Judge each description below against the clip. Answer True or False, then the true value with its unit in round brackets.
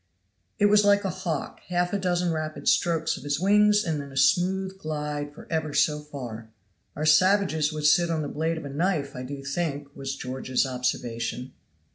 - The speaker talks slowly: False (190 wpm)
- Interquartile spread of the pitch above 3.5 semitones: True (4.0 semitones)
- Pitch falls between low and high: True (155 Hz)